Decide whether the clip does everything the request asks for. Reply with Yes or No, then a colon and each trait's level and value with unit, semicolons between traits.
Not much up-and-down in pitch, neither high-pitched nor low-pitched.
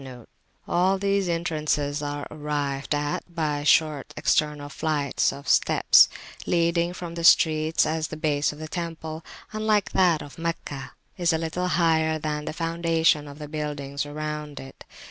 Yes: narrow, 2.3 semitones; medium, 155 Hz